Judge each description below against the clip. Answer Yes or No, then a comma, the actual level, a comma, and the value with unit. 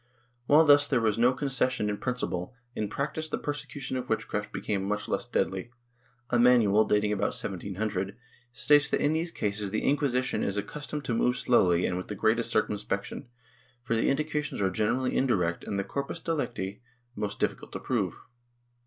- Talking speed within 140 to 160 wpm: No, average, 175 wpm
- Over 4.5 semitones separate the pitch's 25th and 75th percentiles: Yes, average, 5.3 semitones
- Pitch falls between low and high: No, low, 115 Hz